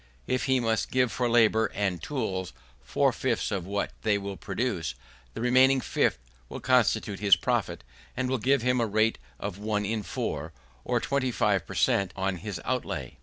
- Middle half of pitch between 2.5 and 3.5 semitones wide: No, average, 4.4 semitones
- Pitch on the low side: Yes, low, 110 Hz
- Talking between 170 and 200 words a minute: Yes, average, 180 wpm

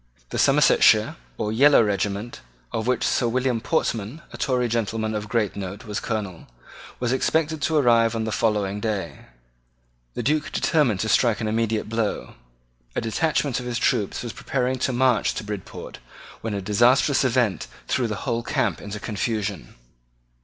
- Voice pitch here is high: No, low, 115 Hz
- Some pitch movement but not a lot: Yes, average, 3.2 semitones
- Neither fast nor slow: Yes, average, 160 wpm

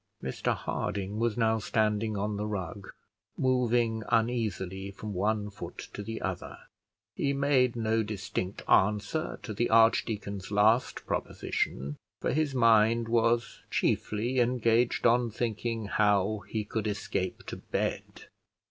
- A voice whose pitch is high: No, low, 110 Hz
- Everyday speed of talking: No, slow, 130 wpm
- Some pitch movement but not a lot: No, narrow, 2.3 semitones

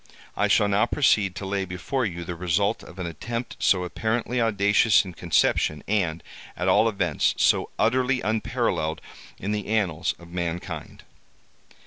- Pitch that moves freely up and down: No, average, 4.2 semitones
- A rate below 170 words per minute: Yes, average, 150 wpm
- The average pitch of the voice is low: Yes, low, 100 Hz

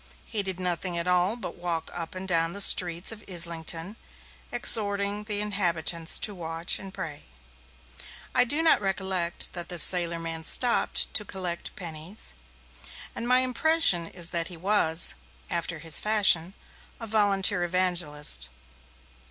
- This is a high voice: No, medium, 180 Hz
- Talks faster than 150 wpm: No, average, 145 wpm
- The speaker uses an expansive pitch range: No, average, 3.3 semitones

